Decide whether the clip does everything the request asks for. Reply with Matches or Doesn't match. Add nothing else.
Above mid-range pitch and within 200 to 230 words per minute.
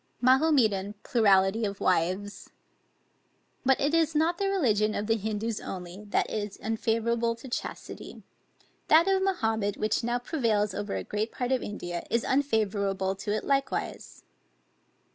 Doesn't match